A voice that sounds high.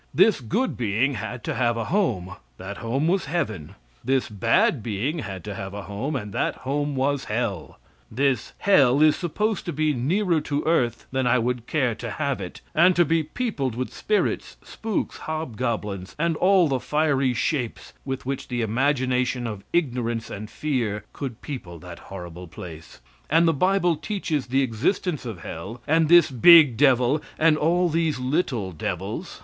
No: low, 130 Hz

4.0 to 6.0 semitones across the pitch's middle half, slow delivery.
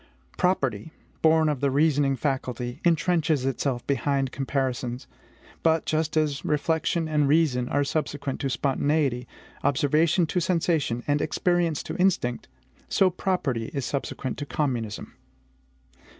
No: average, 3.4 semitones; slow, 120 wpm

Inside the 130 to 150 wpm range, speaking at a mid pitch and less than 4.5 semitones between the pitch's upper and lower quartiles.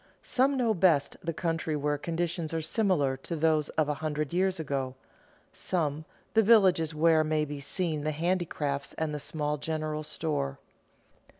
No: average, 160 wpm; medium, 155 Hz; narrow, 2.5 semitones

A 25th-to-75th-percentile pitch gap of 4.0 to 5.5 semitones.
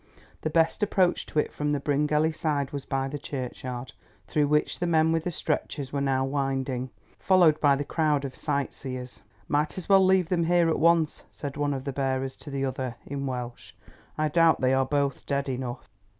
No: average, 3.0 semitones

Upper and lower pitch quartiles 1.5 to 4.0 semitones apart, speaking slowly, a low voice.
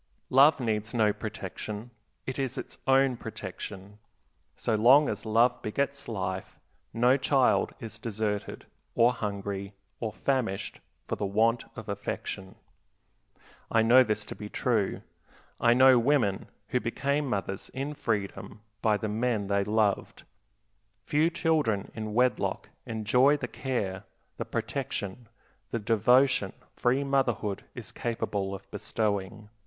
Yes: average, 3.6 semitones; slow, 130 wpm; low, 110 Hz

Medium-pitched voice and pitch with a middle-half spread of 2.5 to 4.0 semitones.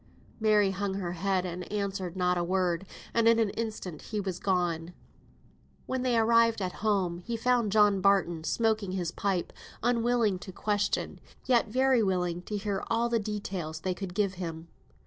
No: high, 195 Hz; average, 3.6 semitones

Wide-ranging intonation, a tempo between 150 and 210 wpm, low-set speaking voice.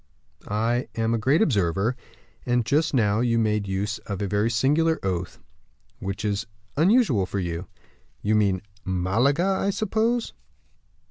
No: wide, 6.0 semitones; average, 140 wpm; low, 110 Hz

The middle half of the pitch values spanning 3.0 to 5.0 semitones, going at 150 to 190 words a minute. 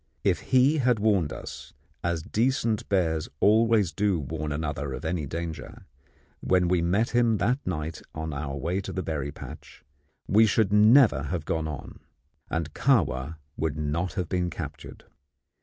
No: wide, 5.4 semitones; average, 160 wpm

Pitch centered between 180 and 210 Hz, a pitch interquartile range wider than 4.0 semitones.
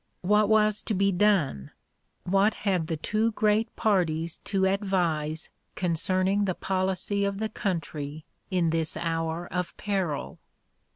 No: medium, 185 Hz; average, 3.7 semitones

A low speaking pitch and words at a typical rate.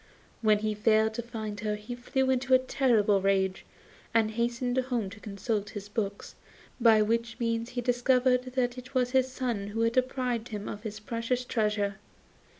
No: high, 230 Hz; average, 175 wpm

